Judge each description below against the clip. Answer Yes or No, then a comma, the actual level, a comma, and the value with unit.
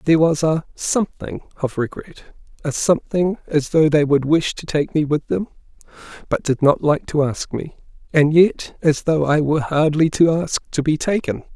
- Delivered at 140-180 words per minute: No, average, 190 wpm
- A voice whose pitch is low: No, medium, 155 Hz